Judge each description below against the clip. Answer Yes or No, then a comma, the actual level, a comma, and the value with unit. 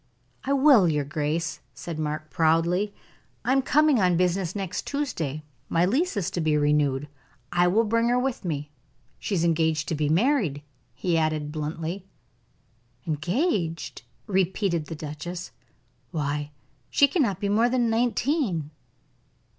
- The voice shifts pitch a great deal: Yes, wide, 6.4 semitones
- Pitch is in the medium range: Yes, medium, 175 Hz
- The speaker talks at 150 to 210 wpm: No, average, 140 wpm